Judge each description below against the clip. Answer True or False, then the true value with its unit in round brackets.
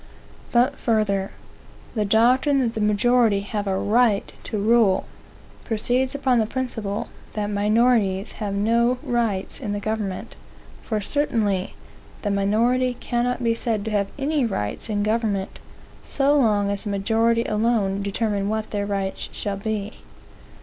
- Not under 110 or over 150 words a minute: True (145 wpm)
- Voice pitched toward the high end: True (215 Hz)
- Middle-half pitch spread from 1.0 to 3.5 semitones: True (2.9 semitones)